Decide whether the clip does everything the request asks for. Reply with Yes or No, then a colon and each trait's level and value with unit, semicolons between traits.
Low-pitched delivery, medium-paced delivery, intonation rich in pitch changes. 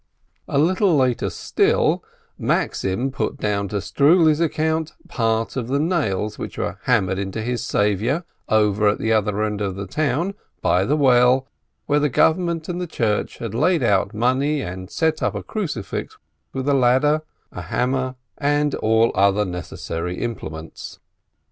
Yes: low, 125 Hz; average, 155 wpm; wide, 6.2 semitones